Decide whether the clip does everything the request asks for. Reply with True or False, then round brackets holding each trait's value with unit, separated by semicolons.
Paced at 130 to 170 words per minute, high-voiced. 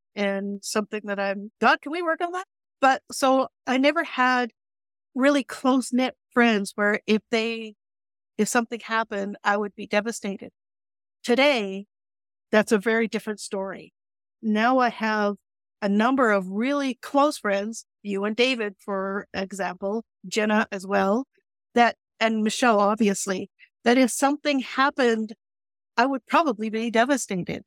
True (140 wpm; 225 Hz)